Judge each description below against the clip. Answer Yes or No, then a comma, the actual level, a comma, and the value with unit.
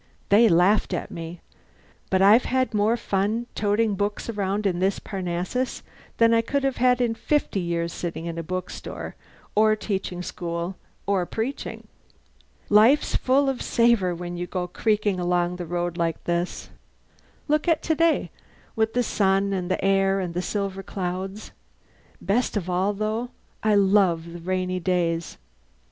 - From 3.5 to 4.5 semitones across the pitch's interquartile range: Yes, average, 3.8 semitones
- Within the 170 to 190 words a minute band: No, average, 155 wpm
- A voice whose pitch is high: Yes, high, 195 Hz